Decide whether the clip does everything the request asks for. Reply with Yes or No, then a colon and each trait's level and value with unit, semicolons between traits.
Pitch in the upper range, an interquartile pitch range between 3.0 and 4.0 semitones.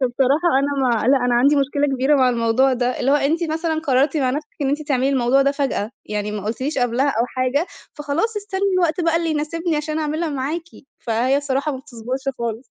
Yes: very high, 275 Hz; average, 3.3 semitones